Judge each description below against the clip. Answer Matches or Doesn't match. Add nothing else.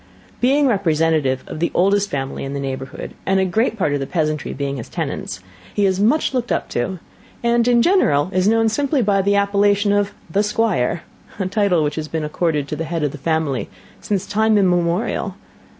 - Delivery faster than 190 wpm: Matches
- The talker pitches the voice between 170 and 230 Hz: Matches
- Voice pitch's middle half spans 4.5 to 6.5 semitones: Matches